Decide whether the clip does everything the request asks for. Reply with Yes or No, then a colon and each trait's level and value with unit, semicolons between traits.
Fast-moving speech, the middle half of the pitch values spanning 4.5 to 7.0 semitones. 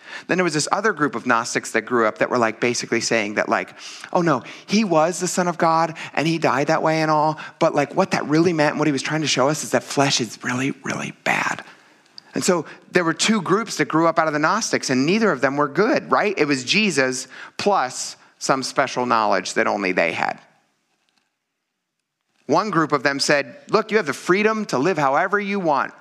Yes: fast, 230 wpm; average, 5.1 semitones